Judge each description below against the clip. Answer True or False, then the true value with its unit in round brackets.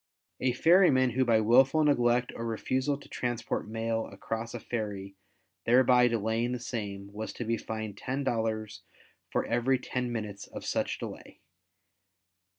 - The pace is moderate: True (145 wpm)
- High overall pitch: False (115 Hz)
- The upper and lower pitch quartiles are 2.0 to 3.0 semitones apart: True (2.5 semitones)